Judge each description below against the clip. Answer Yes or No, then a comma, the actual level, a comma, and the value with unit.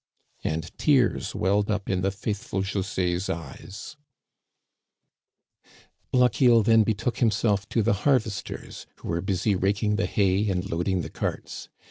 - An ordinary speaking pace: No, slow, 130 wpm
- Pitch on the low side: Yes, low, 100 Hz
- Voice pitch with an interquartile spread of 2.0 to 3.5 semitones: Yes, narrow, 2.5 semitones